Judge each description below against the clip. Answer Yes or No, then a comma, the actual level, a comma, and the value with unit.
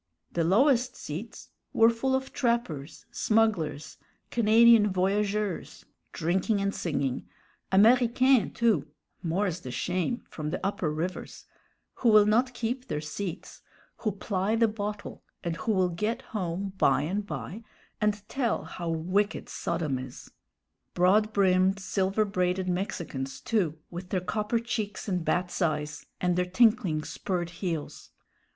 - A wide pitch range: No, average, 4.3 semitones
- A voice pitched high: Yes, high, 195 Hz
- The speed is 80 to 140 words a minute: Yes, slow, 135 wpm